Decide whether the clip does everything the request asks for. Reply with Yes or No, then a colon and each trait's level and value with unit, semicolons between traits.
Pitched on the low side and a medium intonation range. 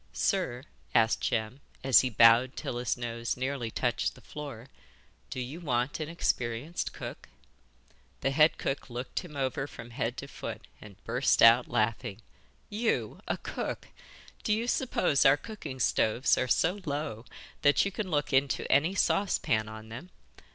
Yes: low, 130 Hz; average, 4.5 semitones